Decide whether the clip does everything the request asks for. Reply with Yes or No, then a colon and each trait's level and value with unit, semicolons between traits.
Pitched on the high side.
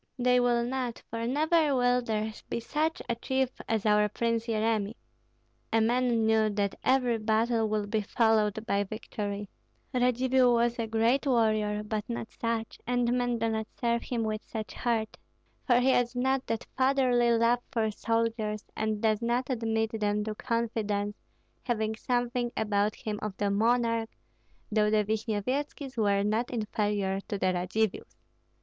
Yes: high, 225 Hz